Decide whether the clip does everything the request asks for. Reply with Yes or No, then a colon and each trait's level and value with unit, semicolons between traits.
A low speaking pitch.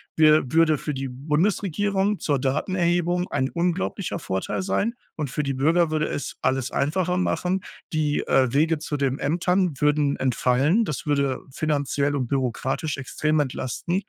No: medium, 150 Hz